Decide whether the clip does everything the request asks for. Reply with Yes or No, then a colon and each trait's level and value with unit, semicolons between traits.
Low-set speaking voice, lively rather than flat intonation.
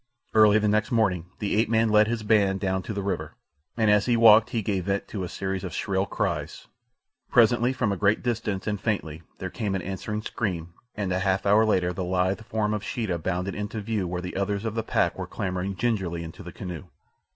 No: low, 100 Hz; average, 2.7 semitones